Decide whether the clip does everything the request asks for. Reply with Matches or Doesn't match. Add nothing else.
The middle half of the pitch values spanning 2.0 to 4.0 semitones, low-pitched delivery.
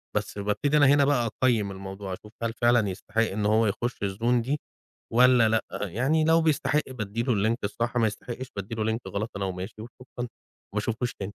Matches